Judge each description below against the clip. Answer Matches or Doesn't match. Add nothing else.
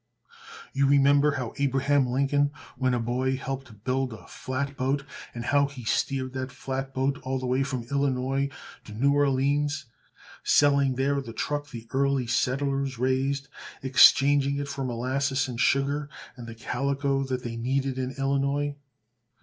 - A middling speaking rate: Matches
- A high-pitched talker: Doesn't match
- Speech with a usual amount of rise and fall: Doesn't match